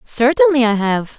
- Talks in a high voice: Yes, very high, 250 Hz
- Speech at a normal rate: Yes, average, 150 wpm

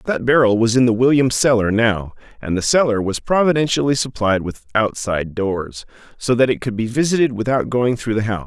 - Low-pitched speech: Yes, low, 120 Hz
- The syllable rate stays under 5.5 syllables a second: No, 5.6 syllables/s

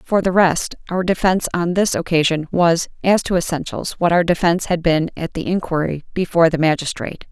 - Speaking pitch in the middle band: Yes, medium, 170 Hz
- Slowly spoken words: No, average, 190 wpm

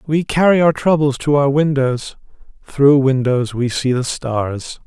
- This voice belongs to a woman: No, male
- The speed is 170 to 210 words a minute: No, average, 160 wpm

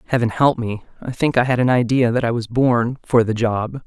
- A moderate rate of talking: No, fast, 250 wpm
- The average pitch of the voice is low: Yes, low, 120 Hz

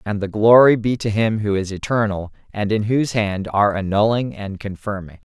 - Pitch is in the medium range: No, low, 105 Hz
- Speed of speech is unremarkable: Yes, average, 190 wpm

